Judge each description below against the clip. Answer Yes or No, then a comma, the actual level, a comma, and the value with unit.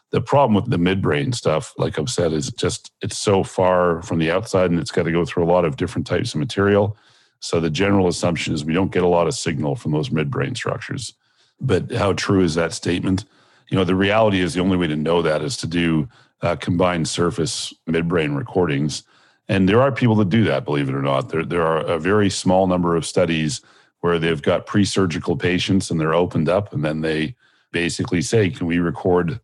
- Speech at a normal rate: No, fast, 220 wpm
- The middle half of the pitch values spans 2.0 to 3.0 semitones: Yes, narrow, 2.5 semitones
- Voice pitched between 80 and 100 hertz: Yes, very low, 90 Hz